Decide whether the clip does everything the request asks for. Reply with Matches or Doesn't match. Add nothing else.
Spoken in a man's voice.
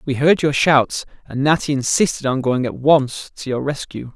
Matches